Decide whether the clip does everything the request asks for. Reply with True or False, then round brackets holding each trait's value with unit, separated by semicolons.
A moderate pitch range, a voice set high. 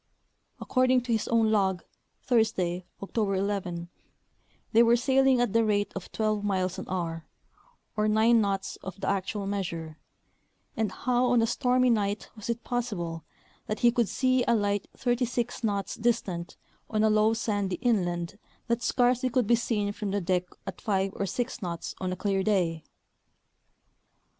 True (3.6 semitones; 210 Hz)